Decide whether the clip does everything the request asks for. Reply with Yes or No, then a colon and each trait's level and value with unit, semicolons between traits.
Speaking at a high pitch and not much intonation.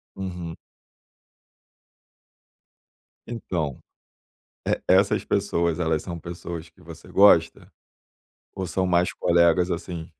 No: very low, 85 Hz; narrow, 1.9 semitones